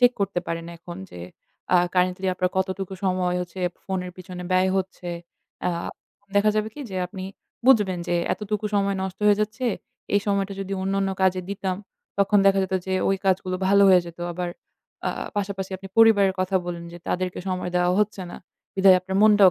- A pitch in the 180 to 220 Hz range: Yes, high, 190 Hz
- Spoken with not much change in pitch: Yes, narrow, 1.5 semitones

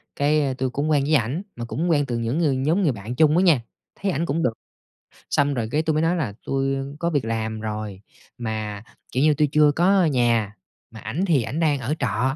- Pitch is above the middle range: No, medium, 140 Hz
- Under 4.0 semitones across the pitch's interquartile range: No, average, 5.1 semitones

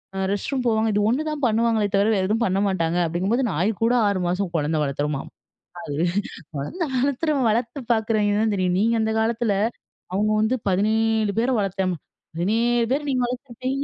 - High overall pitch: Yes, high, 220 Hz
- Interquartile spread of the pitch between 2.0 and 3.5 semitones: No, average, 4.1 semitones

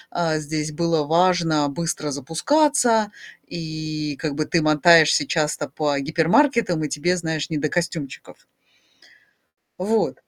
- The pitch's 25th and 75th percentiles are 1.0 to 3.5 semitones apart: Yes, narrow, 2.4 semitones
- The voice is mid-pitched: Yes, medium, 160 Hz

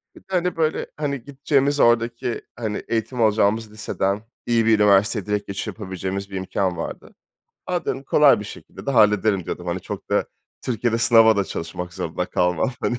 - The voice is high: No, low, 110 Hz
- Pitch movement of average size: Yes, average, 3.6 semitones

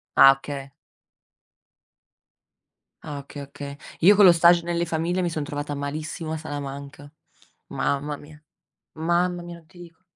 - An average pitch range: Yes, average, 3.2 semitones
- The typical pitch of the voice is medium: Yes, medium, 155 Hz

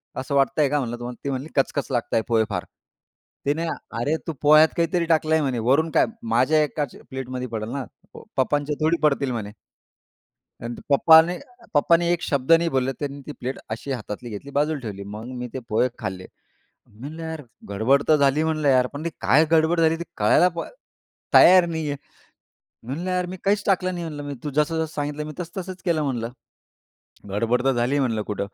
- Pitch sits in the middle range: Yes, medium, 145 Hz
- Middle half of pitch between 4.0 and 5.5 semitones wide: Yes, average, 4.3 semitones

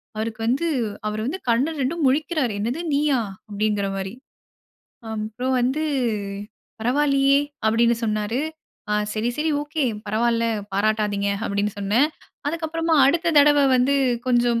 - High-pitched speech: Yes, high, 245 Hz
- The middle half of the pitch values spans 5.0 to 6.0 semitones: Yes, average, 5.3 semitones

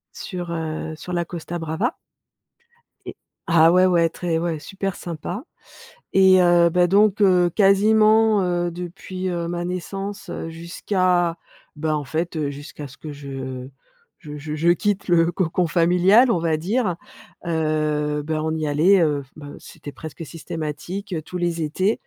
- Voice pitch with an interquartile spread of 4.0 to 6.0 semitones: No, average, 2.9 semitones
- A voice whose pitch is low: No, medium, 170 Hz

